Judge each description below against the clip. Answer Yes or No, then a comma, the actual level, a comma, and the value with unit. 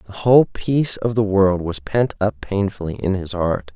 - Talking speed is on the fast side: Yes, fast, 210 wpm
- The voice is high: No, low, 100 Hz